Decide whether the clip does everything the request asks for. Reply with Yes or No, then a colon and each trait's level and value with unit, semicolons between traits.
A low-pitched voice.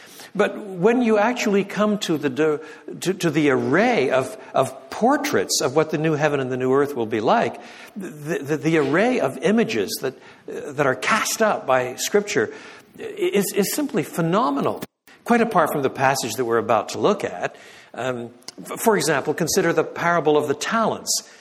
No: medium, 170 Hz